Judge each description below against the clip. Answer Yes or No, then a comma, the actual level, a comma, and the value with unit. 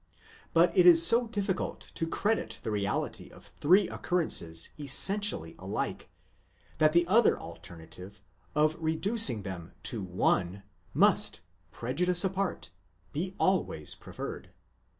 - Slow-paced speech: Yes, slow, 120 wpm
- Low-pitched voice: No, medium, 160 Hz